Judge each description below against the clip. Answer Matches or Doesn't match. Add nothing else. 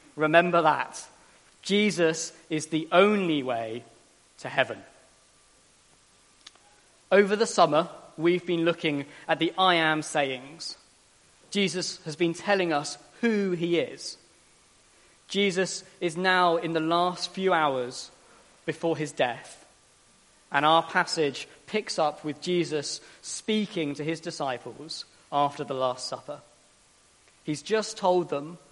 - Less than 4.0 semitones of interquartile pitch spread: Matches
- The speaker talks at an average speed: Doesn't match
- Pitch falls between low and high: Matches